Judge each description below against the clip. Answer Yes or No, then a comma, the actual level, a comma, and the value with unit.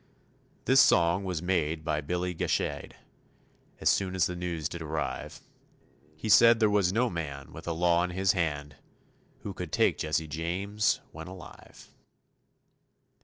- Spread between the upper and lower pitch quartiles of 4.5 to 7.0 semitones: No, average, 3.0 semitones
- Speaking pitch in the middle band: No, very low, 90 Hz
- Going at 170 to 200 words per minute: No, average, 150 wpm